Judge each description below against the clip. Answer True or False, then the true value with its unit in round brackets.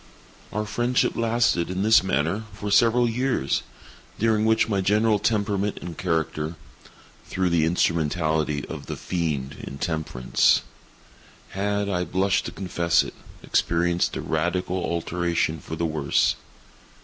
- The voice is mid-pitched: False (90 Hz)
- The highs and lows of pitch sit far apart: False (4.3 semitones)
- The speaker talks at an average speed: False (120 wpm)